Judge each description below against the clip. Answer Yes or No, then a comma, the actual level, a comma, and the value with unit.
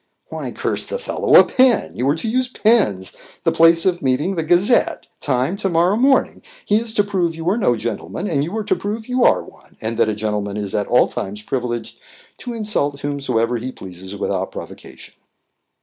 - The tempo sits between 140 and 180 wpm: No, average, 200 wpm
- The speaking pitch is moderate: Yes, medium, 160 Hz